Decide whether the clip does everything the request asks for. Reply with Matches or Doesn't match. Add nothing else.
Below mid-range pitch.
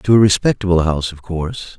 Matches